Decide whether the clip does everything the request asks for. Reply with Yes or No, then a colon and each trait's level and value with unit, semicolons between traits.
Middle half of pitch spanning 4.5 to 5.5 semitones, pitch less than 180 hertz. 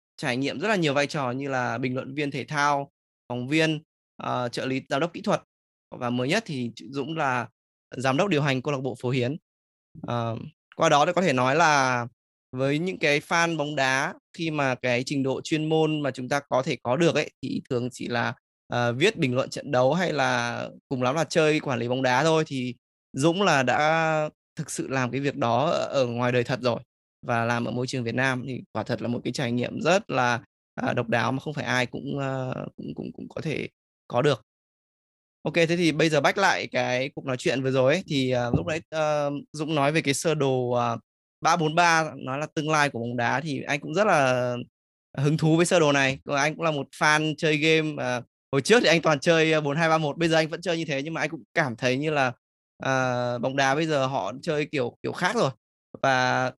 No: average, 3.8 semitones; low, 135 Hz